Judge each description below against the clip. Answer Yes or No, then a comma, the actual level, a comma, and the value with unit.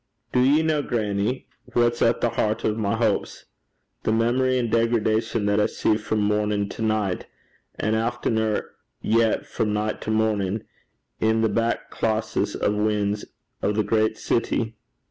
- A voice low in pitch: Yes, low, 110 Hz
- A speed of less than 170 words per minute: Yes, average, 160 wpm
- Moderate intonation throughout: No, narrow, 1.7 semitones